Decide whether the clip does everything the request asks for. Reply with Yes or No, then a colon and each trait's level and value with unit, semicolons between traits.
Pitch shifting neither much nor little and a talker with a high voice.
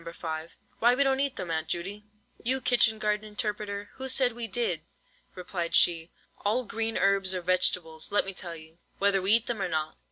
Yes: average, 4.7 semitones; high, 200 Hz